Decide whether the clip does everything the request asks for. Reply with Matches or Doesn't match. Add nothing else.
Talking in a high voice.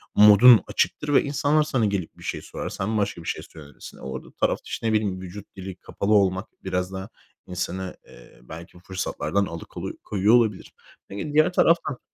Doesn't match